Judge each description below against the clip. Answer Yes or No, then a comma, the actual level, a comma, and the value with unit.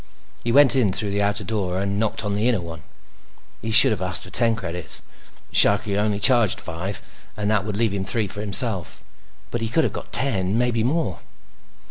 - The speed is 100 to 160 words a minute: No, average, 195 wpm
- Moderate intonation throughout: Yes, average, 3.1 semitones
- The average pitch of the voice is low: Yes, low, 105 Hz